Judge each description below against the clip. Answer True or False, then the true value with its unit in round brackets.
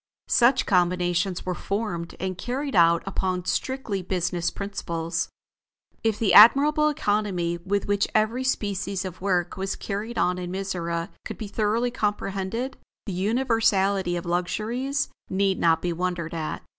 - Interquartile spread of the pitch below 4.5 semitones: True (3.7 semitones)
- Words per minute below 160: True (140 wpm)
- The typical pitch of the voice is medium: False (195 Hz)